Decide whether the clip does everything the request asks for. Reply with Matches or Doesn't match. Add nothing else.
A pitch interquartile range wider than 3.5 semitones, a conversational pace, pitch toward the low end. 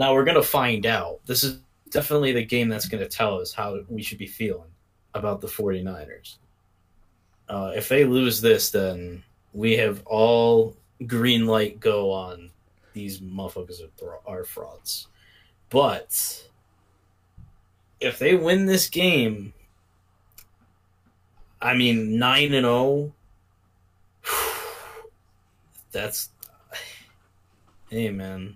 Doesn't match